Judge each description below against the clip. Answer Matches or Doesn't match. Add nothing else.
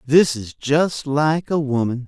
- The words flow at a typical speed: Matches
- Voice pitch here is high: Doesn't match